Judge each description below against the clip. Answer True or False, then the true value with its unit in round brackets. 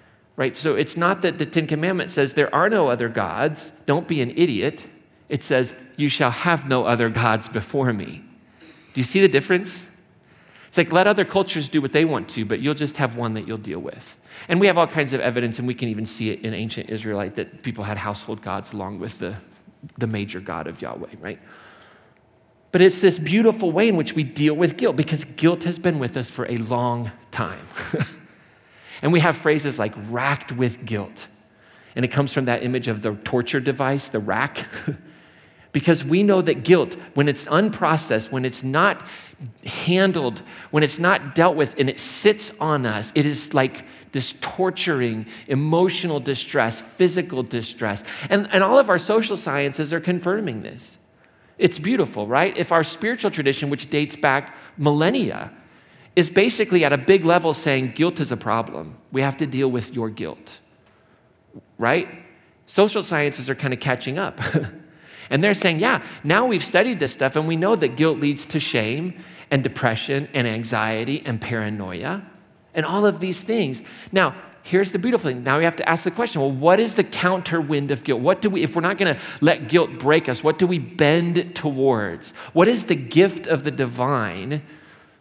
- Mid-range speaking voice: True (145 Hz)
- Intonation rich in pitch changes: True (6.1 semitones)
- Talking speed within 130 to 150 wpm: False (190 wpm)